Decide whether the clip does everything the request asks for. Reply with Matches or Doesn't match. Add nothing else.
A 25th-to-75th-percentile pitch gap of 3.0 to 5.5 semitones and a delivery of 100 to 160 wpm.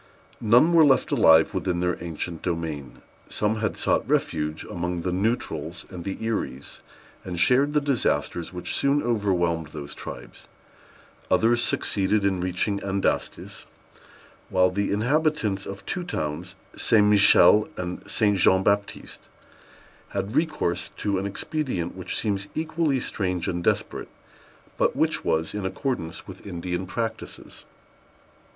Matches